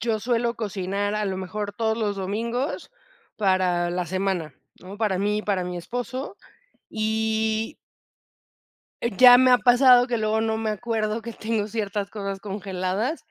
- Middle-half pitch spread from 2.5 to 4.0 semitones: Yes, average, 2.9 semitones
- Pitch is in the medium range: No, high, 215 Hz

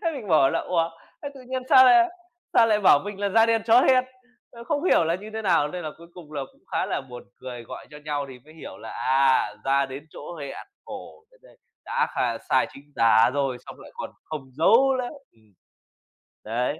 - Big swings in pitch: Yes, wide, 8.9 semitones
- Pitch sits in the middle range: Yes, medium, 165 Hz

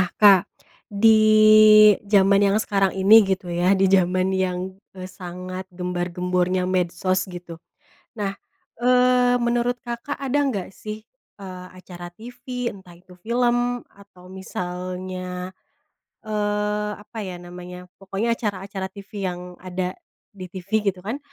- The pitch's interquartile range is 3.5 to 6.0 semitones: No, average, 2.7 semitones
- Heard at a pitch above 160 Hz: Yes, high, 190 Hz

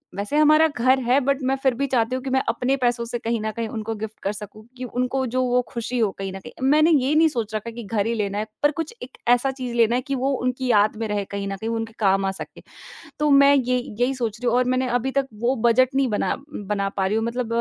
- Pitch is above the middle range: Yes, high, 245 Hz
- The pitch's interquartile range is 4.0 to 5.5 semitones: No, average, 3.3 semitones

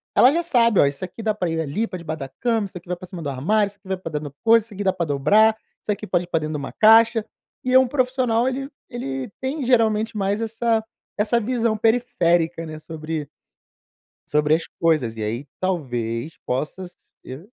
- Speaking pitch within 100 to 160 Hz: No, high, 190 Hz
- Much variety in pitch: Yes, wide, 6.6 semitones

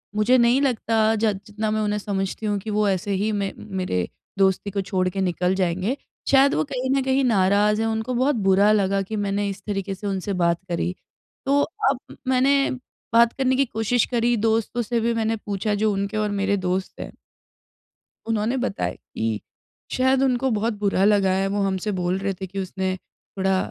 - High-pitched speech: Yes, high, 210 Hz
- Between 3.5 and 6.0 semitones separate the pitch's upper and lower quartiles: No, average, 3.1 semitones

